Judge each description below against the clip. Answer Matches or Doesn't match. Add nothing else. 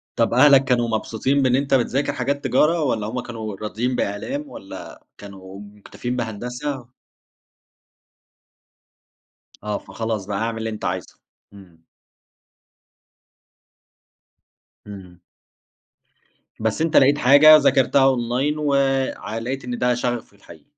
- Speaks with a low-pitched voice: Matches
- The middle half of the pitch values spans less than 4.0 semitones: Doesn't match